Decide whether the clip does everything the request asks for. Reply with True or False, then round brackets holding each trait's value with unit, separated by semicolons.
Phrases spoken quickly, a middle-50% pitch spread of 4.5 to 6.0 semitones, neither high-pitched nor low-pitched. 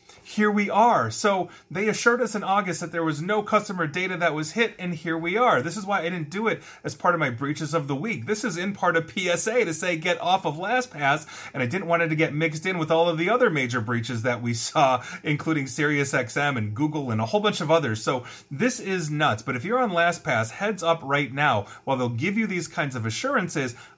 True (250 wpm; 5.0 semitones; 165 Hz)